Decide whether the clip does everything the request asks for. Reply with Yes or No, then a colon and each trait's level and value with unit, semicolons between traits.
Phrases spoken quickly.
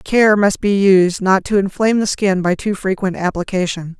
No: average, 195 wpm